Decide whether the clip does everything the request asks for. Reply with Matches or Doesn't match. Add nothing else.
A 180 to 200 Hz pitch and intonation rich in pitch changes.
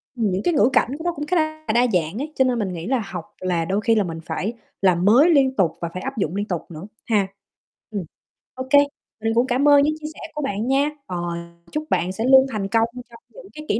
Doesn't match